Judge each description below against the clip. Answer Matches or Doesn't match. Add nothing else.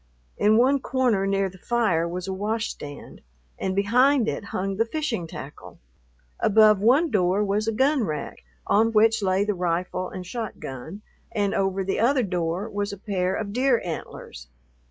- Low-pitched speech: Doesn't match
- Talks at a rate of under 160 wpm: Doesn't match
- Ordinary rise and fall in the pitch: Matches